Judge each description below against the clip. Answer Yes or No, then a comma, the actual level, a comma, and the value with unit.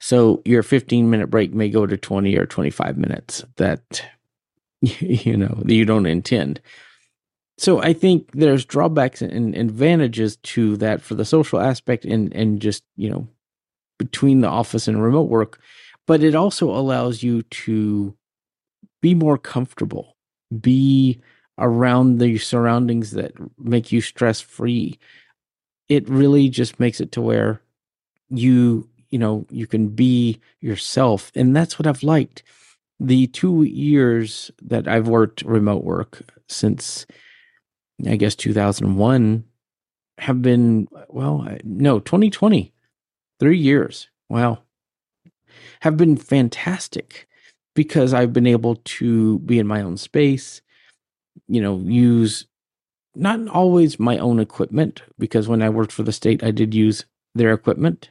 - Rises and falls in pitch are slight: No, average, 3.9 semitones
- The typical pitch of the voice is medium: No, low, 120 Hz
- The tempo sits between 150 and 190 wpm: No, slow, 135 wpm